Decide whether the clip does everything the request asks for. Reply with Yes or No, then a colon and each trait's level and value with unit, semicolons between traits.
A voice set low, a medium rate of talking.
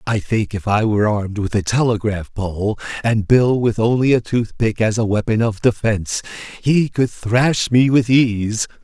Yes: low, 110 Hz; average, 190 wpm